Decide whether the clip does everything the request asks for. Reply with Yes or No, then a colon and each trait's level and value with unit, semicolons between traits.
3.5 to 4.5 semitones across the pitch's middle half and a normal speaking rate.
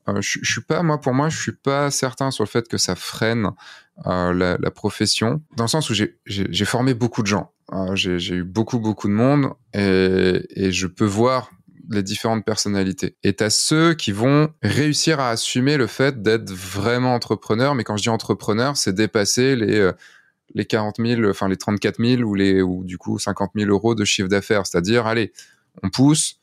Yes: average, 4.1 semitones; average, 210 wpm